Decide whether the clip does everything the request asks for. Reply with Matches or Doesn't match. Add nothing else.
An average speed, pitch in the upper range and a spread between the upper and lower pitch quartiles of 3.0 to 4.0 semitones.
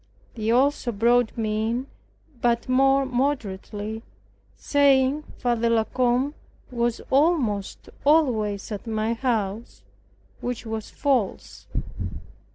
Doesn't match